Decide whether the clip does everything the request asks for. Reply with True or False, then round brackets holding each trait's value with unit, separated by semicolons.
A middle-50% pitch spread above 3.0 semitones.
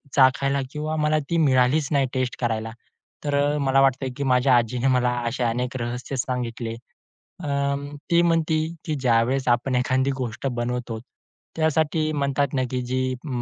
False (2.6 semitones)